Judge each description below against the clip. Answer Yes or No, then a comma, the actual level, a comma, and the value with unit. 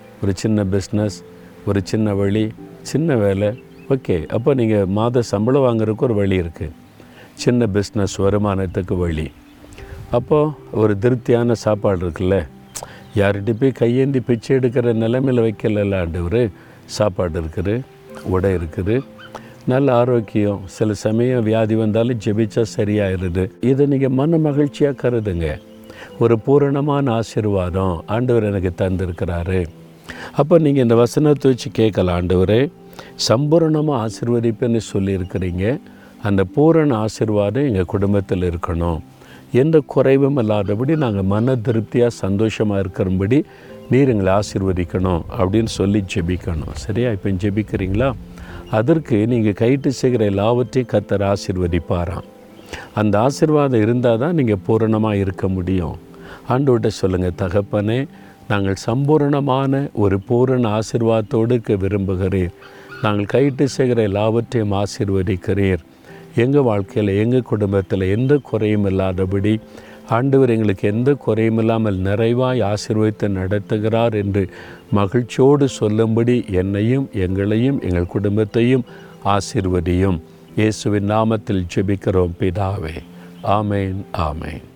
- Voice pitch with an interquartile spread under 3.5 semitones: No, average, 4.2 semitones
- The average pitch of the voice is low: Yes, low, 105 Hz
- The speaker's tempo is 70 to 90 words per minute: No, average, 105 wpm